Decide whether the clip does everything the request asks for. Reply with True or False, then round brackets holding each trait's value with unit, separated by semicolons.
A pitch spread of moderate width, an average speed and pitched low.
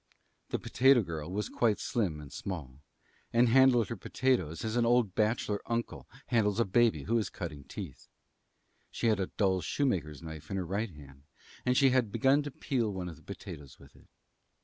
False (6.3 semitones; 190 wpm; 105 Hz)